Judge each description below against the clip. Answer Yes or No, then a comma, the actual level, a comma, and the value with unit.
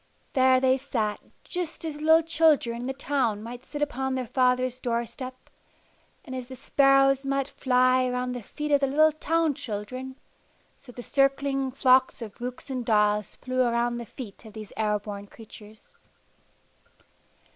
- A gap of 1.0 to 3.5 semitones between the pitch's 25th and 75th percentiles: Yes, narrow, 2.6 semitones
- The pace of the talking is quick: No, average, 165 wpm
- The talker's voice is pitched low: No, very high, 255 Hz